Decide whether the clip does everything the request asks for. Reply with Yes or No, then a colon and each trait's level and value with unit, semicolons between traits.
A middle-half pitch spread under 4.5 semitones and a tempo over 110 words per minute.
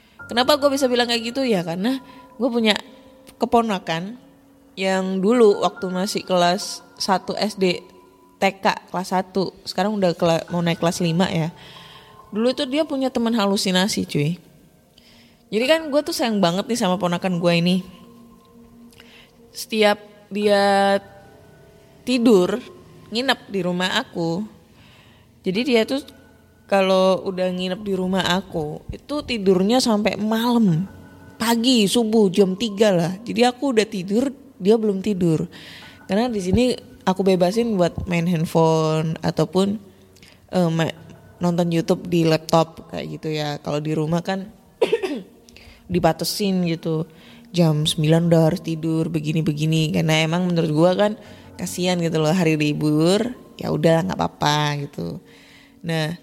No: average, 5.0 semitones; average, 130 wpm